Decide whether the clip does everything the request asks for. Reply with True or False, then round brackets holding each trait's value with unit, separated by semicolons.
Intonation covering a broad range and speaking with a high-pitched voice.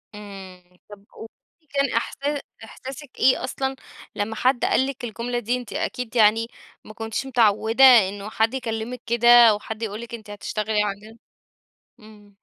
False (3.1 semitones; 225 Hz)